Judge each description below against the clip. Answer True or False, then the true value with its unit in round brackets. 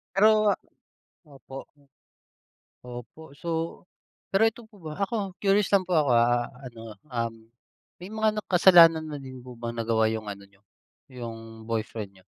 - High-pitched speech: False (125 Hz)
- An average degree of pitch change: False (7.8 semitones)